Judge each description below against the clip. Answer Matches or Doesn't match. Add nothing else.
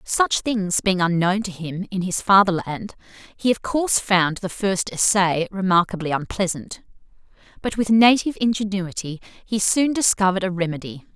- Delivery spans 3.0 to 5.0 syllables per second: Matches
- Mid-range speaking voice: Doesn't match